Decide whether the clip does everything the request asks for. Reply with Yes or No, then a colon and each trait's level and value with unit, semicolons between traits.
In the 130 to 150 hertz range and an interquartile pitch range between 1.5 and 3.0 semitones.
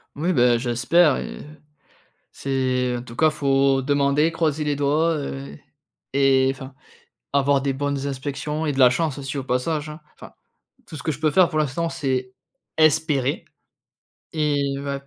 Yes: medium, 140 Hz; narrow, 2.4 semitones